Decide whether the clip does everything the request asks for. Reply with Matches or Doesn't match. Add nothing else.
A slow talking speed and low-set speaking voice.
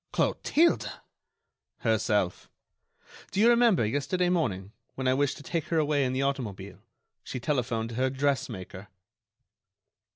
Matches